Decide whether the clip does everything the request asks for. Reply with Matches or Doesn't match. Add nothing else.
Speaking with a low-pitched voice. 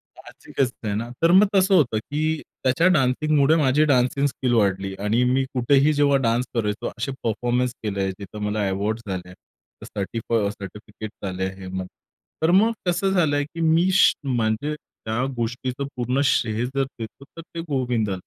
Matches